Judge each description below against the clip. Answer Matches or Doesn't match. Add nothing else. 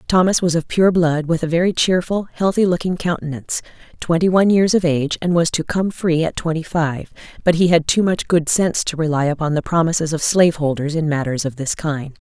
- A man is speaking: Doesn't match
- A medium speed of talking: Doesn't match